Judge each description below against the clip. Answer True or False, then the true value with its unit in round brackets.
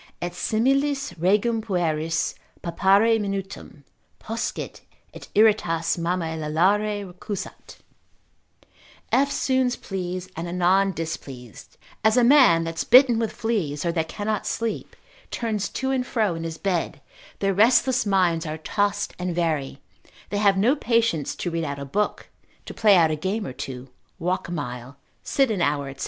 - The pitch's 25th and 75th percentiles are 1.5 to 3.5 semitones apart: False (5.2 semitones)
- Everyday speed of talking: True (150 wpm)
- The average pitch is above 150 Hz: True (190 Hz)